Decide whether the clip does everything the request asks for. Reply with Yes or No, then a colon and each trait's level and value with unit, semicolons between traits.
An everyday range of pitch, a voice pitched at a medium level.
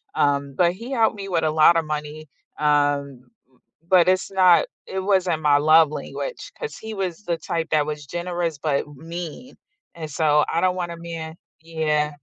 Yes: average, 3.2 semitones; medium, 165 Hz